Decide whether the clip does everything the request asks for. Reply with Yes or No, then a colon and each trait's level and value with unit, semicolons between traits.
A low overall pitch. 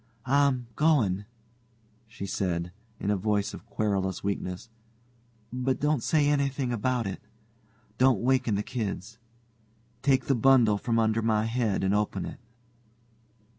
Yes: low, 115 Hz